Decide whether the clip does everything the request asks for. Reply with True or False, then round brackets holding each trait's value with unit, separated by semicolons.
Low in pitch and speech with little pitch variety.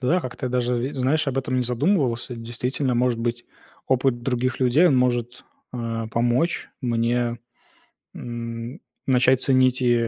True (125 Hz; 1.6 semitones)